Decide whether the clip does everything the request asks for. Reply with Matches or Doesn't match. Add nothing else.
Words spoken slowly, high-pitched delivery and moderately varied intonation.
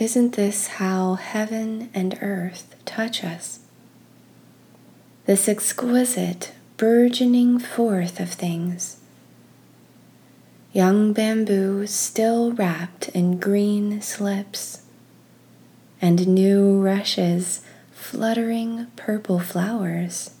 Matches